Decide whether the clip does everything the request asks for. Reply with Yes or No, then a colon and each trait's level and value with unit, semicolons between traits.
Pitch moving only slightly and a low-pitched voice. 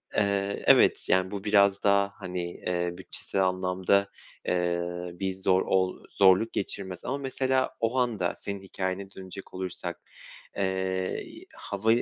Yes: narrow, 1.4 semitones; very low, 95 Hz